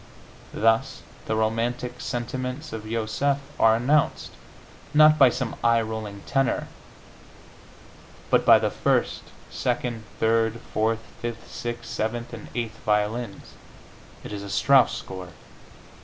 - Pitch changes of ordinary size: No, narrow, 2.0 semitones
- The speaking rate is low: Yes, slow, 120 wpm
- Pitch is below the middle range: Yes, low, 115 Hz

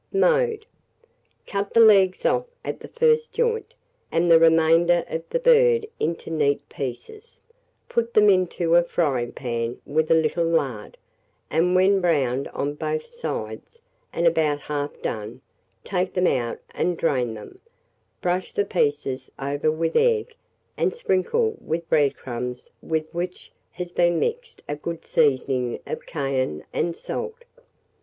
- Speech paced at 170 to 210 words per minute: No, average, 140 wpm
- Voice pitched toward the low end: No, medium, 170 Hz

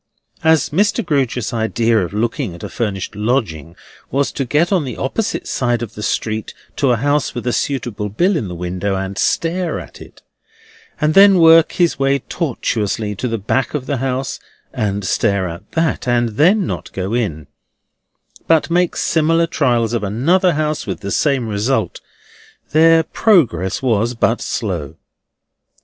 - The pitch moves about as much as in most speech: No, wide, 6.8 semitones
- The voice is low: Yes, low, 125 Hz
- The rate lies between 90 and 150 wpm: No, average, 165 wpm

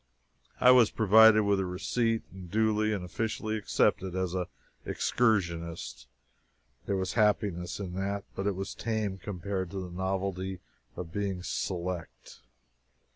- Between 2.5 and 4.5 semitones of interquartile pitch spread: Yes, average, 2.9 semitones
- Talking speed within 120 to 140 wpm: Yes, slow, 135 wpm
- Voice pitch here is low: Yes, very low, 95 Hz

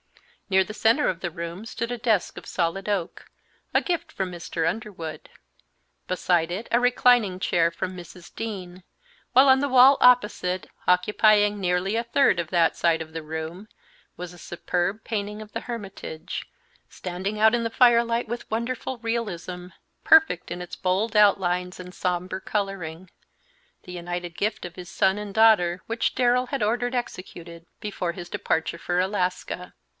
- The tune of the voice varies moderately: Yes, average, 4.3 semitones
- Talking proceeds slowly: No, average, 160 wpm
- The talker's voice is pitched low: No, high, 190 Hz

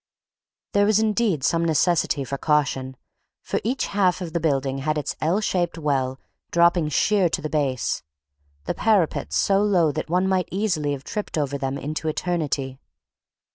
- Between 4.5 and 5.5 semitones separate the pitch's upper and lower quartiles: Yes, average, 4.8 semitones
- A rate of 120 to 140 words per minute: No, average, 165 wpm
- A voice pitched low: No, medium, 160 Hz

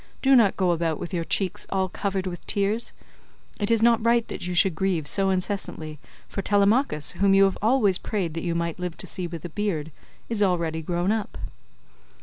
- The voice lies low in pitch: No, high, 190 Hz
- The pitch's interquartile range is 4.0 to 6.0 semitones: No, average, 3.4 semitones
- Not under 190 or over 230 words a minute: Yes, average, 195 wpm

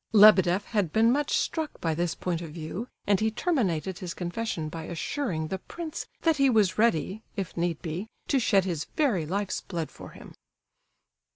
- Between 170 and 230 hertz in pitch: Yes, high, 190 Hz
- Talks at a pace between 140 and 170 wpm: No, average, 180 wpm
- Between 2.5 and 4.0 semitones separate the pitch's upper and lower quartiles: No, average, 5.1 semitones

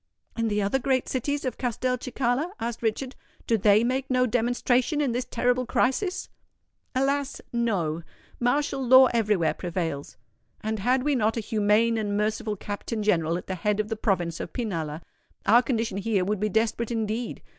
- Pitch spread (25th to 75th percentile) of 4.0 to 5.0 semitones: No, average, 3.4 semitones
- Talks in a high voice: Yes, high, 230 Hz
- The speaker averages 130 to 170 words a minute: Yes, average, 165 wpm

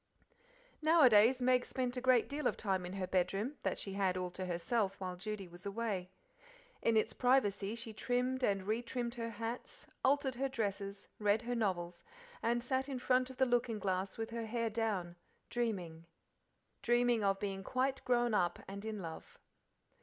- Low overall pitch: No, high, 225 Hz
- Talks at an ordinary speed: Yes, average, 170 wpm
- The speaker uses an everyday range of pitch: Yes, average, 4.2 semitones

